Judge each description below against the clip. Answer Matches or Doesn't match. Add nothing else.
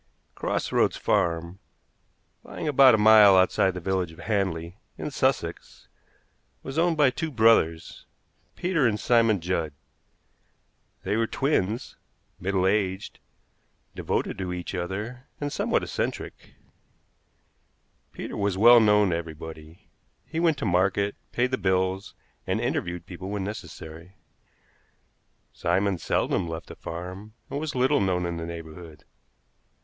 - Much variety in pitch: Doesn't match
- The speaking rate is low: Matches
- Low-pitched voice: Matches